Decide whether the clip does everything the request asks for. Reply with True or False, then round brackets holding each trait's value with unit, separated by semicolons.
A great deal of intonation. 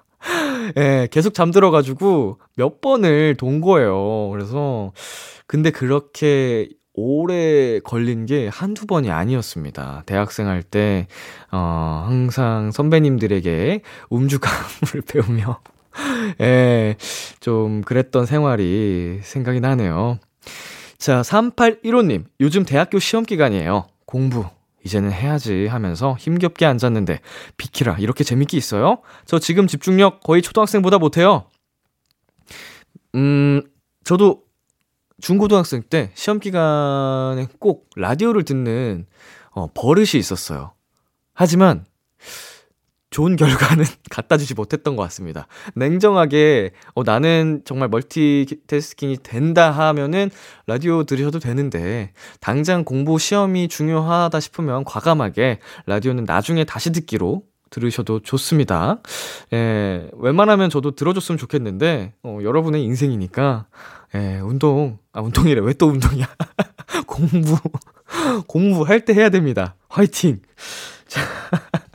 True (6.6 semitones)